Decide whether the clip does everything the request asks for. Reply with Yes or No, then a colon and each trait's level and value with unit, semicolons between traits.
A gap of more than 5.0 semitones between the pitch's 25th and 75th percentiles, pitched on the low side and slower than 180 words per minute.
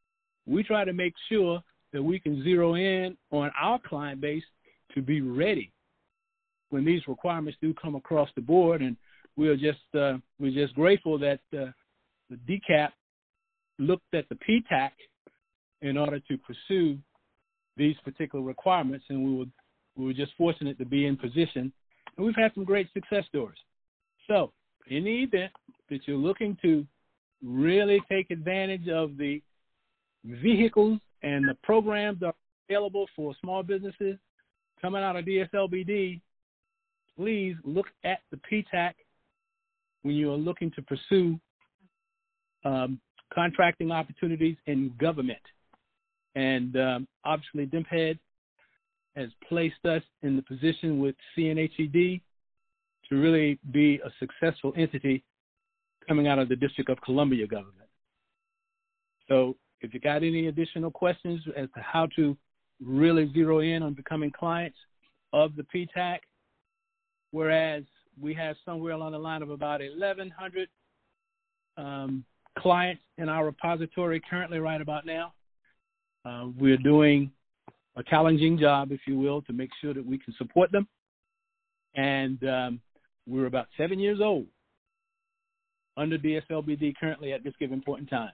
No: wide, 5.4 semitones; medium, 160 Hz; average, 140 wpm